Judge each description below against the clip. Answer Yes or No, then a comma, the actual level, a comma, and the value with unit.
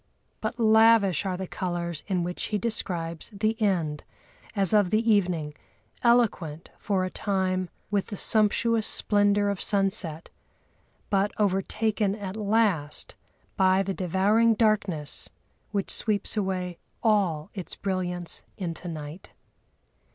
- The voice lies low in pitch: No, high, 195 Hz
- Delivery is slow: Yes, slow, 120 wpm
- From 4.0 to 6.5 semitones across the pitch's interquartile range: No, average, 3.1 semitones